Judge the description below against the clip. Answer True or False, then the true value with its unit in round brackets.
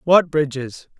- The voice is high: False (150 Hz)